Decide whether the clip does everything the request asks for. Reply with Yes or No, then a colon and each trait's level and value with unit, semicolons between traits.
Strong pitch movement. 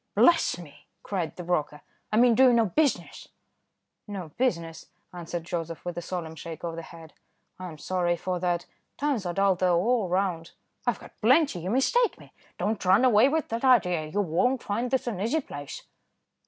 Yes: wide, 6.1 semitones